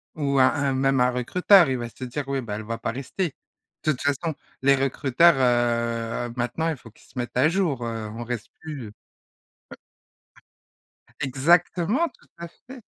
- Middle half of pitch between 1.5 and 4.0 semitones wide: No, average, 4.7 semitones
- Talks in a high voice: No, low, 135 Hz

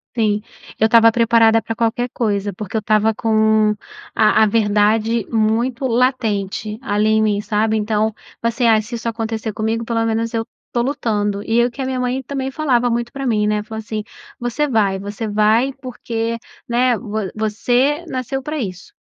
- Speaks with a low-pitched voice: No, high, 225 Hz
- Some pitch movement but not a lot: No, narrow, 2.1 semitones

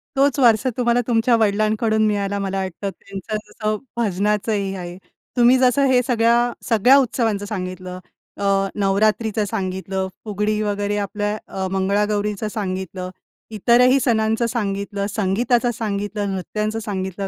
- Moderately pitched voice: No, high, 210 Hz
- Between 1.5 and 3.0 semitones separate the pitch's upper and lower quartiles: Yes, narrow, 2.5 semitones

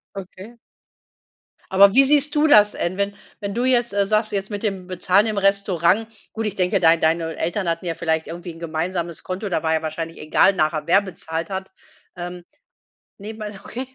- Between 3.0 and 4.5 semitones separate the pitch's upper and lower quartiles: Yes, average, 3.6 semitones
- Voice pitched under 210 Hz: Yes, high, 190 Hz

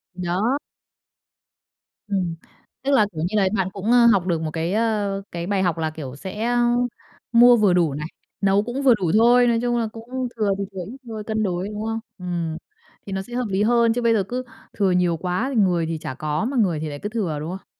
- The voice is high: Yes, high, 200 Hz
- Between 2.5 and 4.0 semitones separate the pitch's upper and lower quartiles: No, average, 4.9 semitones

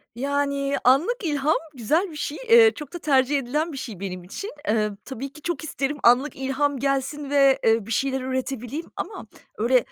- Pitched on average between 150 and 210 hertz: No, very high, 275 Hz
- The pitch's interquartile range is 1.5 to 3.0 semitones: Yes, narrow, 2.6 semitones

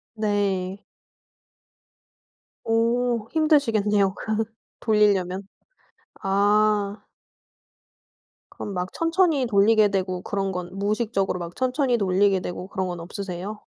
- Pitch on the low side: No, high, 205 Hz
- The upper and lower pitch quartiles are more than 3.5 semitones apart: No, average, 2.9 semitones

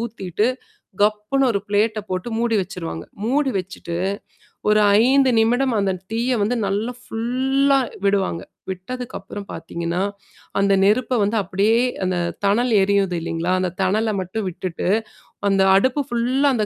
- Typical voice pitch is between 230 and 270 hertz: No, high, 210 Hz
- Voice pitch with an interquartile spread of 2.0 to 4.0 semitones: No, average, 4.4 semitones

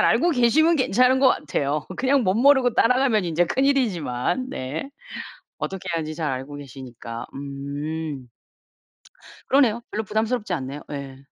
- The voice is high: No, medium, 180 Hz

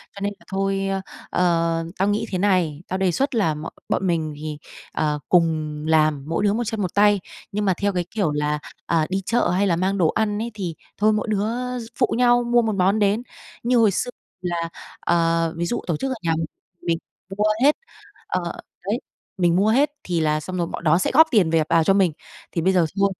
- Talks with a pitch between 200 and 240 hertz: No, medium, 185 Hz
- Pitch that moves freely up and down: No, average, 3.8 semitones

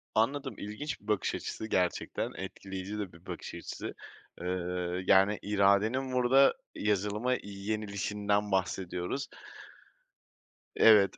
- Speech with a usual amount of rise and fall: No, narrow, 2.1 semitones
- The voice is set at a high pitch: No, low, 105 Hz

